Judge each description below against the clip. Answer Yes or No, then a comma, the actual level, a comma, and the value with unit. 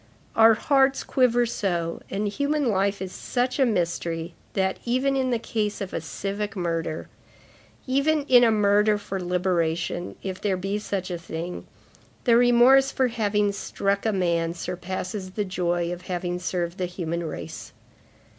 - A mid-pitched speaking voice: No, high, 195 Hz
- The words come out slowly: No, average, 155 wpm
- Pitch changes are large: No, average, 4.9 semitones